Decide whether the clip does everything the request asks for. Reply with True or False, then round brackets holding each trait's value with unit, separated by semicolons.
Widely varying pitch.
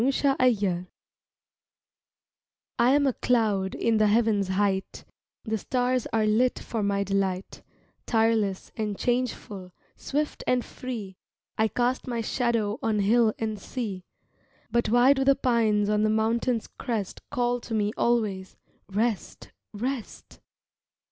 False (3.1 semitones)